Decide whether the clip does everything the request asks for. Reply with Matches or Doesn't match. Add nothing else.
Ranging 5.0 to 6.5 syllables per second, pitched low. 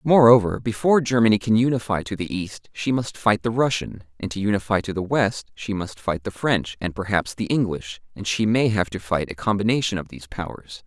Matches